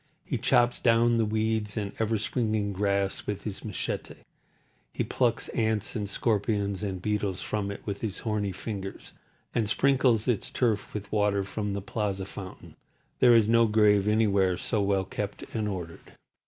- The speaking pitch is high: No, low, 105 Hz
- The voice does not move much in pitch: Yes, narrow, 1.9 semitones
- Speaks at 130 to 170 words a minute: Yes, average, 165 wpm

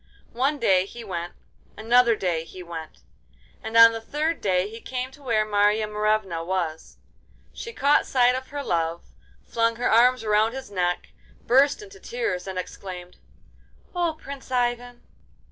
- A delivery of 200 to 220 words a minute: No, average, 155 wpm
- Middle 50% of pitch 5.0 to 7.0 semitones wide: Yes, wide, 5.5 semitones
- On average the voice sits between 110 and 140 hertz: No, high, 225 Hz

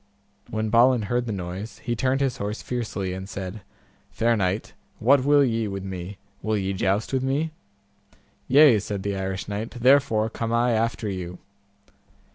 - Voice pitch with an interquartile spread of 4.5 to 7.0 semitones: No, average, 3.9 semitones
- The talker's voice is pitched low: Yes, low, 110 Hz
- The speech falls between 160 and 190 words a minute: Yes, average, 165 wpm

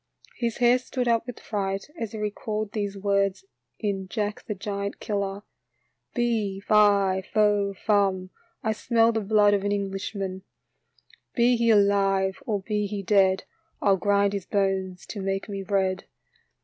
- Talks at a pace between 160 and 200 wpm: Yes, average, 165 wpm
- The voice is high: Yes, high, 200 Hz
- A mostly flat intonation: Yes, narrow, 1.7 semitones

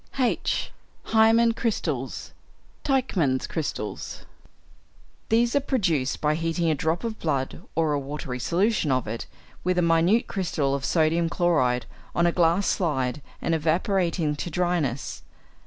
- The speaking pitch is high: No, medium, 165 Hz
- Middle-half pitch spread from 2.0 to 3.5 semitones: No, average, 4.7 semitones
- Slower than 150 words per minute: Yes, slow, 135 wpm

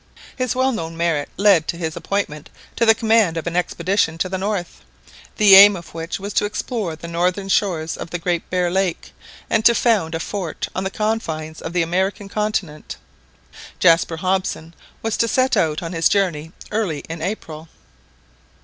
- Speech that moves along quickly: No, average, 180 wpm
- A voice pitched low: No, medium, 180 Hz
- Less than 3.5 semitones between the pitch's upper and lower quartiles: No, average, 3.9 semitones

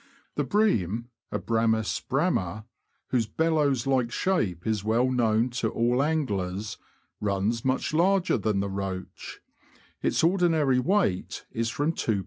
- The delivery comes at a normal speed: No, slow, 125 wpm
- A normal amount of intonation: No, wide, 5.9 semitones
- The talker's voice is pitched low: Yes, low, 115 Hz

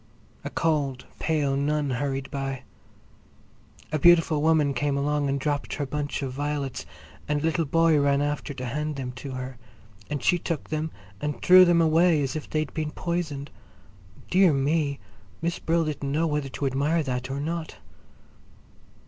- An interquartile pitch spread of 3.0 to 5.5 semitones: No, narrow, 2.5 semitones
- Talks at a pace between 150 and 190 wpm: Yes, average, 165 wpm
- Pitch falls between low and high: Yes, medium, 145 Hz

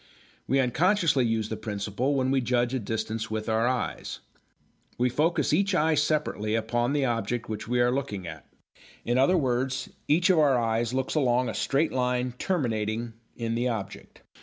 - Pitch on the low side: Yes, low, 125 Hz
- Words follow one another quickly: No, average, 175 wpm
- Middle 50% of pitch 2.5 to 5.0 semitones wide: Yes, average, 3.5 semitones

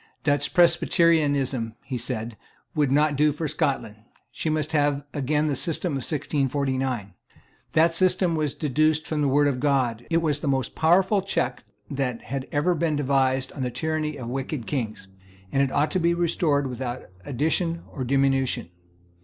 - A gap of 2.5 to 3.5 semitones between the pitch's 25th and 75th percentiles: Yes, average, 3.0 semitones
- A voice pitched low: No, medium, 145 Hz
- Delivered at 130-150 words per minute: No, average, 165 wpm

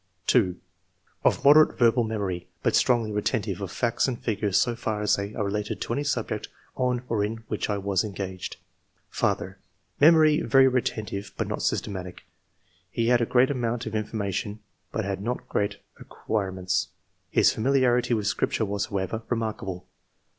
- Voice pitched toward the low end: Yes, low, 110 Hz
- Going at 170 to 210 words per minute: Yes, average, 175 wpm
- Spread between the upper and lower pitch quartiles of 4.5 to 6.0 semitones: No, average, 3.4 semitones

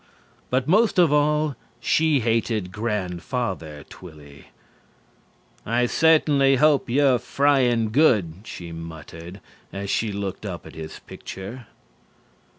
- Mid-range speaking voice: No, low, 115 Hz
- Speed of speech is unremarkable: No, slow, 110 wpm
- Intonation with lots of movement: Yes, wide, 7.5 semitones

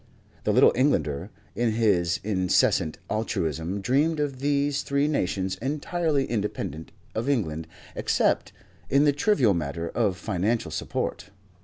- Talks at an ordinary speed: No, slow, 125 wpm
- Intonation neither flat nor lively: No, wide, 7.7 semitones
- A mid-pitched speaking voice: No, low, 110 Hz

